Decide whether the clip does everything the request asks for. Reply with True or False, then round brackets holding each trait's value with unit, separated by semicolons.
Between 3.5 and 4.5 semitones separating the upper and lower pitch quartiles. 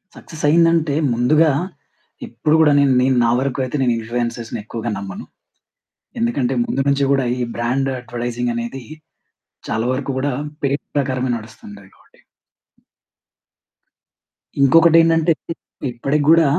True (3.9 semitones)